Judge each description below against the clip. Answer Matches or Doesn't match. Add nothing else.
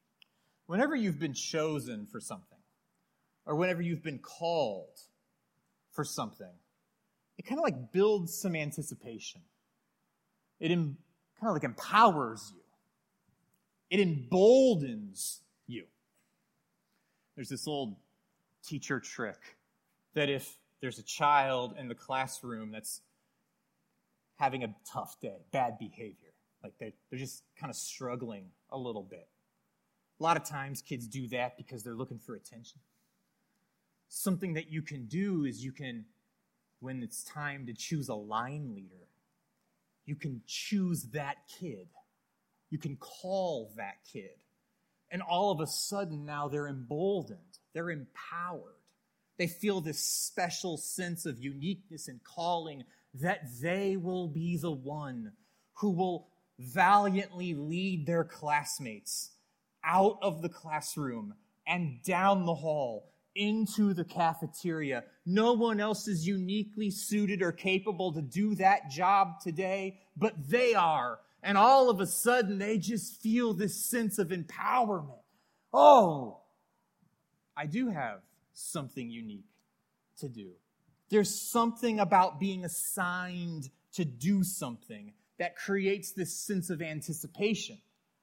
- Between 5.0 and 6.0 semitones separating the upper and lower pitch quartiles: Matches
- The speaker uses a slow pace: Matches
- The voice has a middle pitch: Matches